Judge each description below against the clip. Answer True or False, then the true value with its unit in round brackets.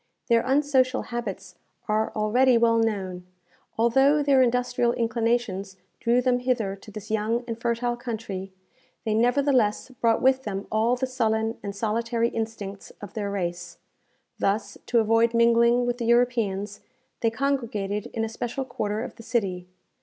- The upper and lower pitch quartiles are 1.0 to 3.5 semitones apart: True (2.6 semitones)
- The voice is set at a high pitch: True (230 Hz)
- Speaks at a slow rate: False (150 wpm)